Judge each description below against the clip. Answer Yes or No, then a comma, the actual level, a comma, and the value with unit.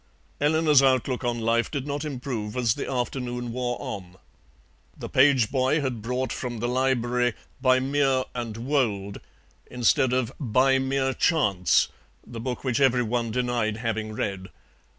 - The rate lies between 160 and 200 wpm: No, average, 150 wpm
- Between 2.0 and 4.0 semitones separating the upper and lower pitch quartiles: Yes, narrow, 2.5 semitones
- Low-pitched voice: Yes, low, 125 Hz